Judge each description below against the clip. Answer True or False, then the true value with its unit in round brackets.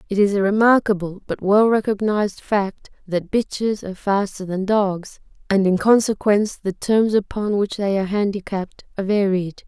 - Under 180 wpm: True (160 wpm)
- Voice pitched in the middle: False (200 Hz)